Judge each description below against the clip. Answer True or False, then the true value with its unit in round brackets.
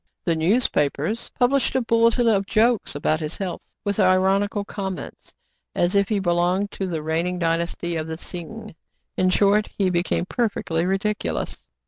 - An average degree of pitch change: True (3.6 semitones)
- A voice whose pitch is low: False (190 Hz)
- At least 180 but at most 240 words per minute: False (150 wpm)